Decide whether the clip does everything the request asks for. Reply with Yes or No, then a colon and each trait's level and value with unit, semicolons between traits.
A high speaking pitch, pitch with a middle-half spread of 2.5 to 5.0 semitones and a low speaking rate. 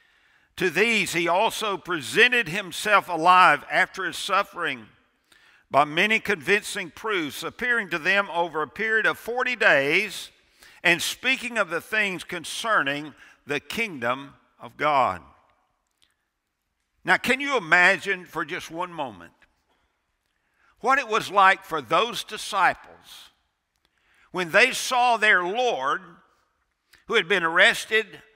Yes: high, 195 Hz; average, 4.5 semitones; slow, 120 wpm